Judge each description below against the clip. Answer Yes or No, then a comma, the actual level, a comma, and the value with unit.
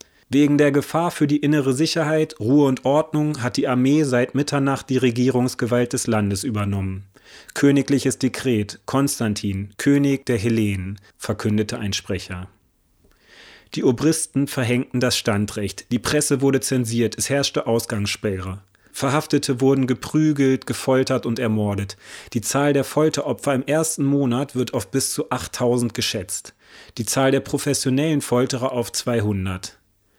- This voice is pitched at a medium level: No, low, 130 Hz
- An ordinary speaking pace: Yes, average, 135 wpm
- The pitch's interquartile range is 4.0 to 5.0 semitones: Yes, average, 4.4 semitones